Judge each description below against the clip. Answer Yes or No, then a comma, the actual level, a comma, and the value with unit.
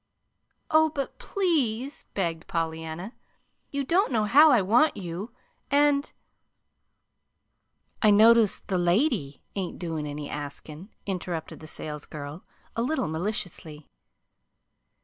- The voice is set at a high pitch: Yes, high, 195 Hz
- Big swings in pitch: Yes, wide, 8.5 semitones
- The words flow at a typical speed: No, slow, 110 wpm